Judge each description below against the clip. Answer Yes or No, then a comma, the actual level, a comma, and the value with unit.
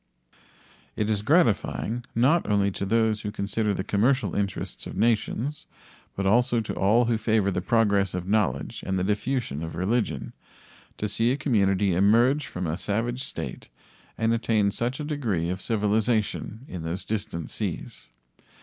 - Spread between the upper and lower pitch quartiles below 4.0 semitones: Yes, average, 3.1 semitones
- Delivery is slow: No, average, 160 wpm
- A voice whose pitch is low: Yes, low, 105 Hz